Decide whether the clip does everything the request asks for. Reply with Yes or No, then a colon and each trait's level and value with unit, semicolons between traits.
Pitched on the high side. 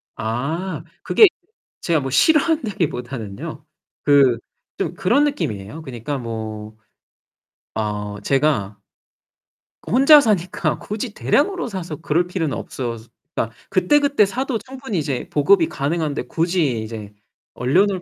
No: medium, 155 Hz